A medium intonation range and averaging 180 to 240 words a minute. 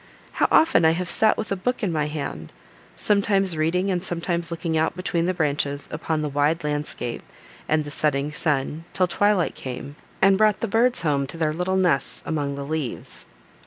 Yes: average, 3.9 semitones; average, 190 wpm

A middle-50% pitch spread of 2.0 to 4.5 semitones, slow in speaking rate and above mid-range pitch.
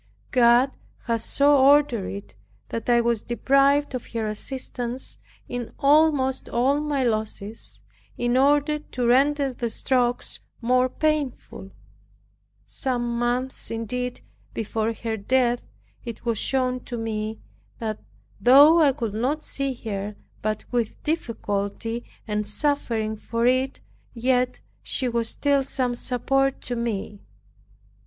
Yes: average, 3.0 semitones; slow, 125 wpm; high, 245 Hz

